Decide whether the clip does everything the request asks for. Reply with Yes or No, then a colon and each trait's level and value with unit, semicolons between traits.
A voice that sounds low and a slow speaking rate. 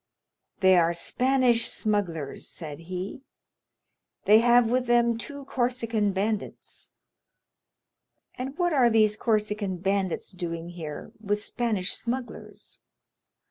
No: high, 215 Hz; slow, 105 wpm